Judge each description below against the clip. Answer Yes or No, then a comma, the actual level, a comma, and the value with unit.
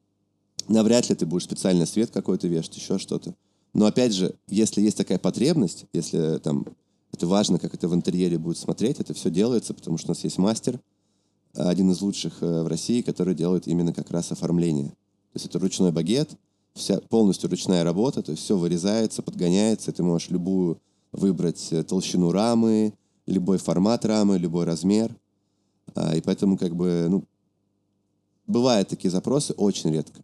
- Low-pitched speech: Yes, very low, 95 Hz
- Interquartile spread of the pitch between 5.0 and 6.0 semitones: No, average, 2.7 semitones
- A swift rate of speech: Yes, fast, 165 wpm